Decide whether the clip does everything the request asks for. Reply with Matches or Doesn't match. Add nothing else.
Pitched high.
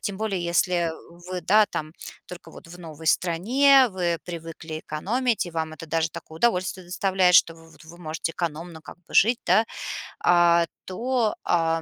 Doesn't match